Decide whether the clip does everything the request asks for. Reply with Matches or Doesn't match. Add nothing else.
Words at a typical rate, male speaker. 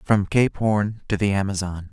Matches